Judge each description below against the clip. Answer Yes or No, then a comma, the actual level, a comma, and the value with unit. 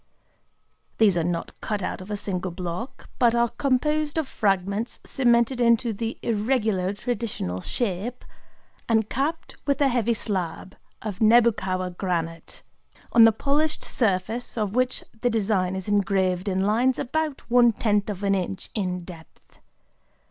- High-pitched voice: Yes, high, 215 Hz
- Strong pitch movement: No, average, 4.4 semitones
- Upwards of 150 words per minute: No, average, 145 wpm